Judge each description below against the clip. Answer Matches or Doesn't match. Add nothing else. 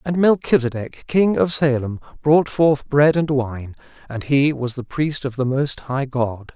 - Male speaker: Matches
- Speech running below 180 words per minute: Doesn't match